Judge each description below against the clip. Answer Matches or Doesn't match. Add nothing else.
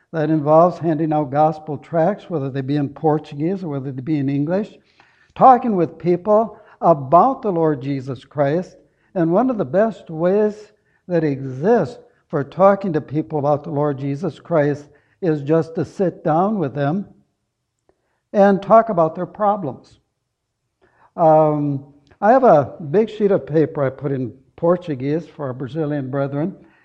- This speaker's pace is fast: Doesn't match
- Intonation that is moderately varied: Matches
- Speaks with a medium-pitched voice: Matches